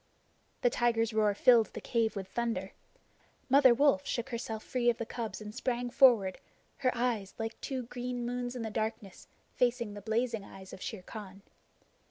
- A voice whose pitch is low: No, high, 230 Hz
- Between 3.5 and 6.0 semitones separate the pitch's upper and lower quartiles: No, narrow, 2.5 semitones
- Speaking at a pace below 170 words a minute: No, average, 175 wpm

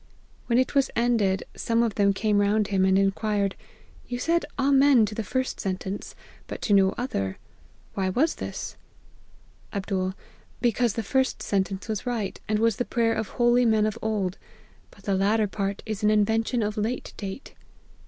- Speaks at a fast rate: No, average, 185 wpm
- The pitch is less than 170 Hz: No, high, 215 Hz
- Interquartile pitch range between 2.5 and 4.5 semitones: Yes, average, 3.3 semitones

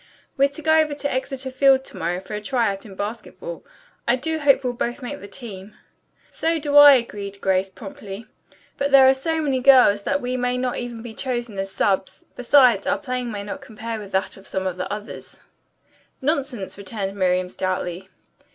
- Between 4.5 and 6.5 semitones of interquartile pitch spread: Yes, wide, 5.5 semitones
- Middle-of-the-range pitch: No, high, 240 Hz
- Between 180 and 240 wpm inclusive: Yes, average, 195 wpm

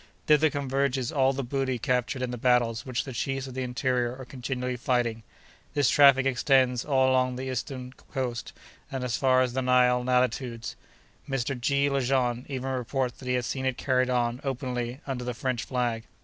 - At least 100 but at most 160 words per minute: No, average, 185 wpm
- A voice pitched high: No, low, 130 Hz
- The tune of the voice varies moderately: No, narrow, 1.4 semitones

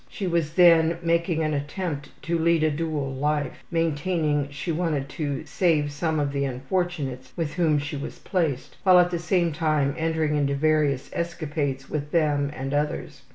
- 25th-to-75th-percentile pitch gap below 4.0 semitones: Yes, average, 2.7 semitones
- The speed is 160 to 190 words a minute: Yes, average, 170 wpm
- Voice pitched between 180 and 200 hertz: No, medium, 155 Hz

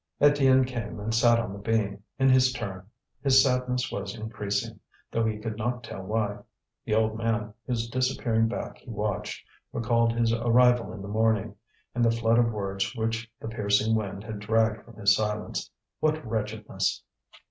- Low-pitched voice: Yes, low, 115 Hz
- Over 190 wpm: No, average, 170 wpm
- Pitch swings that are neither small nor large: No, narrow, 2.1 semitones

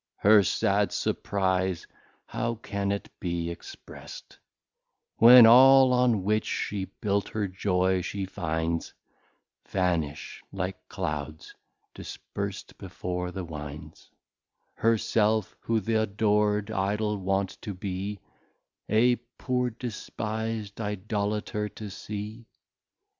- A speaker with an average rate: No, slow, 100 wpm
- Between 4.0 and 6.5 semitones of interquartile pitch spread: No, average, 3.0 semitones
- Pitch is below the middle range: Yes, low, 100 Hz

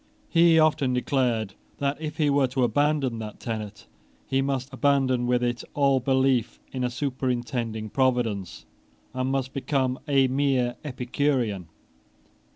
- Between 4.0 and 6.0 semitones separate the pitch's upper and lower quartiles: No, narrow, 2.4 semitones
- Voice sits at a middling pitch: No, low, 130 Hz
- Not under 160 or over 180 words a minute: No, slow, 135 wpm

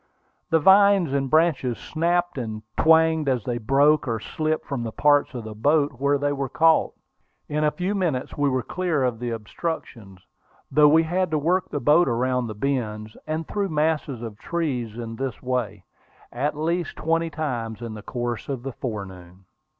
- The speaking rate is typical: Yes, average, 180 wpm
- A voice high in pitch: No, medium, 140 Hz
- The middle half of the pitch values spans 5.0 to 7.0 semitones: Yes, average, 5.3 semitones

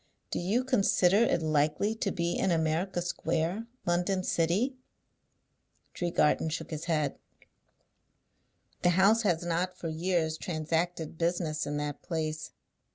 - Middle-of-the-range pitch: Yes, medium, 170 Hz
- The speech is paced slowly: Yes, slow, 125 wpm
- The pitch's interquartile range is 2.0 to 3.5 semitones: Yes, average, 2.7 semitones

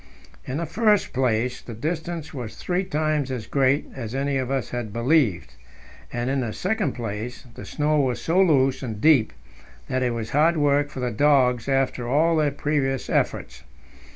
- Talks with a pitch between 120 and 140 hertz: Yes, low, 135 Hz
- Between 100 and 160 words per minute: No, average, 180 wpm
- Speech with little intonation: No, average, 3.8 semitones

